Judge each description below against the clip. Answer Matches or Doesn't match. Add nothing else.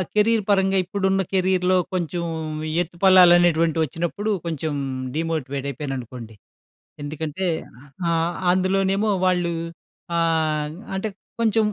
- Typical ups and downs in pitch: Matches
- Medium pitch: Matches